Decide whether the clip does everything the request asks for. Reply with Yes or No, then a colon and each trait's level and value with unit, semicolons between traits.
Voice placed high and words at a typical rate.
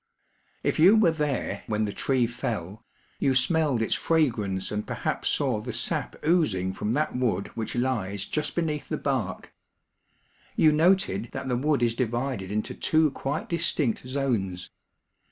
No: low, 125 Hz; average, 155 wpm